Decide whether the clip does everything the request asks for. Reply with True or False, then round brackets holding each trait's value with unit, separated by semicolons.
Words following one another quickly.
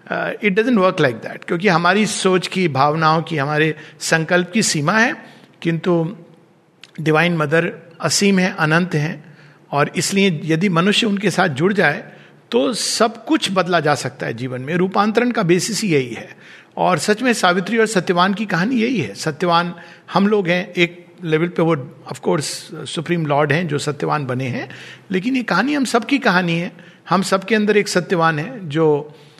False (175 wpm)